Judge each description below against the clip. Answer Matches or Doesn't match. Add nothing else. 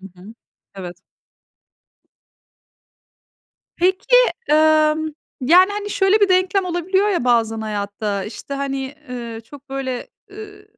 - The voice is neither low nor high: Doesn't match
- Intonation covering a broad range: Matches